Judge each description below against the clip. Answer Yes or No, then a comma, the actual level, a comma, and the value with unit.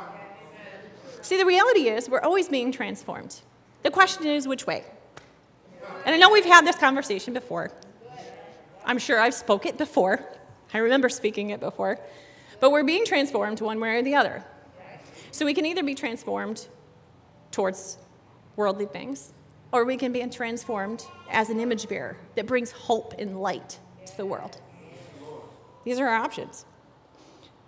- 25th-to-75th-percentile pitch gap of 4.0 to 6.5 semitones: Yes, average, 5.1 semitones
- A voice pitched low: No, high, 240 Hz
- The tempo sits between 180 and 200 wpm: No, average, 155 wpm